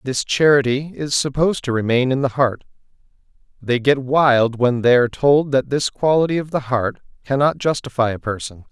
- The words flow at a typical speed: Yes, average, 180 wpm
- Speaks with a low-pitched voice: Yes, low, 130 Hz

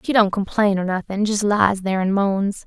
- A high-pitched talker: Yes, high, 200 Hz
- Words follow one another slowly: No, fast, 205 wpm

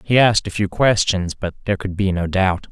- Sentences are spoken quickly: Yes, fast, 245 wpm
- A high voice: No, very low, 95 Hz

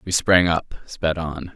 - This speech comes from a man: Yes, male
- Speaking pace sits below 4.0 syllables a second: Yes, 3.6 syllables/s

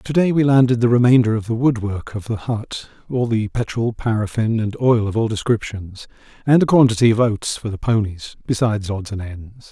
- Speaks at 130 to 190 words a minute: No, fast, 205 wpm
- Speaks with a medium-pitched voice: No, low, 115 Hz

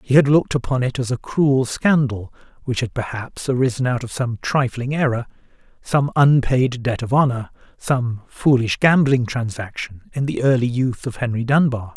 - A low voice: Yes, low, 125 Hz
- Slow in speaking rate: No, average, 170 wpm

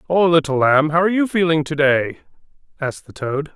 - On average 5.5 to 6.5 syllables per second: Yes, 5.7 syllables/s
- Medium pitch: Yes, medium, 155 Hz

